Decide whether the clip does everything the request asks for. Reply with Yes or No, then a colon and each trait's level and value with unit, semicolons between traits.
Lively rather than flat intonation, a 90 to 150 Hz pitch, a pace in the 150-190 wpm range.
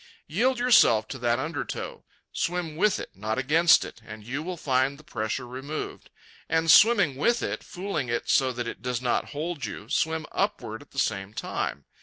Yes: wide, 5.9 semitones; medium, 140 Hz; average, 185 wpm